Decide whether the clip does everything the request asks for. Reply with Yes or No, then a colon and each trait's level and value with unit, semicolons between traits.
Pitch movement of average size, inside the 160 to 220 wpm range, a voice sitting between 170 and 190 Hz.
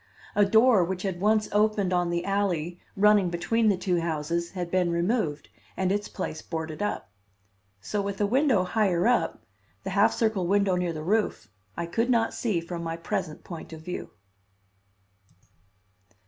Yes: average, 3.5 semitones; average, 165 wpm; medium, 185 Hz